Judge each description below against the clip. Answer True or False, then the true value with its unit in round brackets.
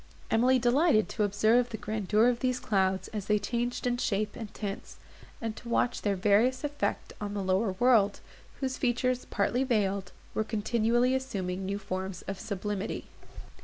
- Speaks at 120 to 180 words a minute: True (165 wpm)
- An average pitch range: True (3.5 semitones)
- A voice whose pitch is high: True (215 Hz)